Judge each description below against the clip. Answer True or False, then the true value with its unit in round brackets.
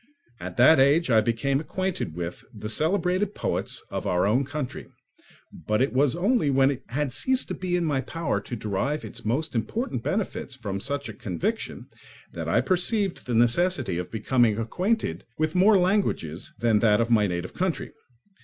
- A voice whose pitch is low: True (130 Hz)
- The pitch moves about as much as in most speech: False (8.2 semitones)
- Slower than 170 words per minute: False (175 wpm)